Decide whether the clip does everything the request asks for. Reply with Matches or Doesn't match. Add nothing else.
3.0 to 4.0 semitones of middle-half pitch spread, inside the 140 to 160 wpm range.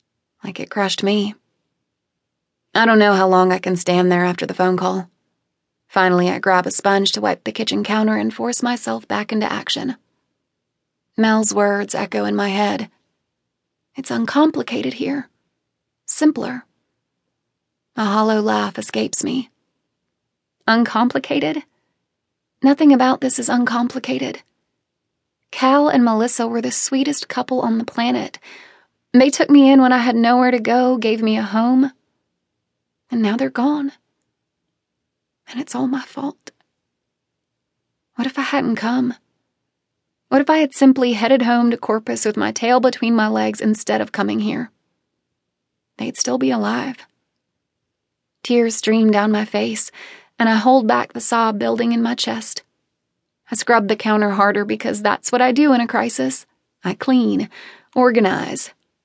Matches